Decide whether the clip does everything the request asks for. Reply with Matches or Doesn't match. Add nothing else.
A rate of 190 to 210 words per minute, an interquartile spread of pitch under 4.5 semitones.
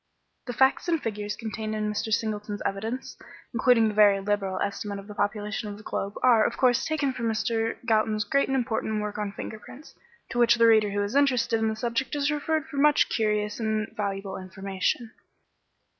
Matches